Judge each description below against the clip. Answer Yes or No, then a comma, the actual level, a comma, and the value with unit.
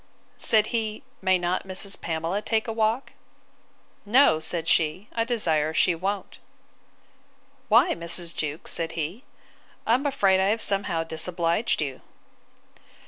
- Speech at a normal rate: No, slow, 130 wpm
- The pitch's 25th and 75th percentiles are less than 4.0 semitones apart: No, average, 4.9 semitones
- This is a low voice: No, high, 190 Hz